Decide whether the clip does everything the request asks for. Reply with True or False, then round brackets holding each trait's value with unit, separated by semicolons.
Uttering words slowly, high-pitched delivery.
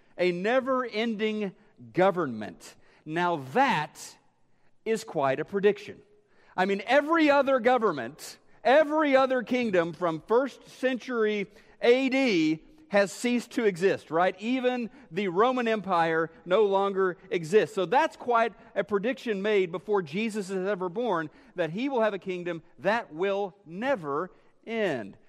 True (130 wpm; 210 Hz)